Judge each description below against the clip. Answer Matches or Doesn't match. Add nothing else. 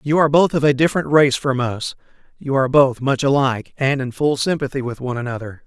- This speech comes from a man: Matches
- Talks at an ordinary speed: Doesn't match